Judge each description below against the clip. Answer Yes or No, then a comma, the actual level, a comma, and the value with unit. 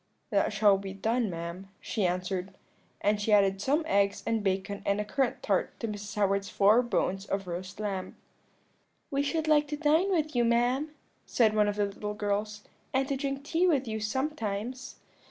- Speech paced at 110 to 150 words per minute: No, average, 185 wpm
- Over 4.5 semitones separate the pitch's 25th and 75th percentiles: Yes, average, 5.0 semitones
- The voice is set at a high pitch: Yes, high, 210 Hz